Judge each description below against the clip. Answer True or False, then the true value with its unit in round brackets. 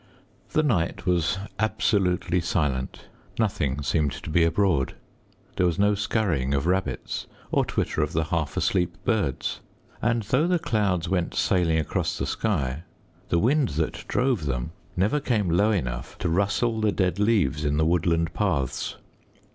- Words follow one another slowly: False (155 wpm)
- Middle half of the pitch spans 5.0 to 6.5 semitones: True (5.3 semitones)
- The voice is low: True (90 Hz)